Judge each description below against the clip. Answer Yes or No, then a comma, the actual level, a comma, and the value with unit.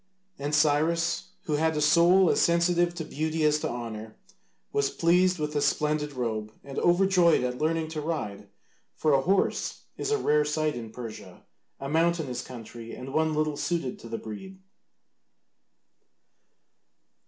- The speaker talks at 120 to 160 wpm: Yes, average, 155 wpm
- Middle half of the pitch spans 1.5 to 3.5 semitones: No, average, 4.8 semitones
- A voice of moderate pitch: Yes, medium, 150 Hz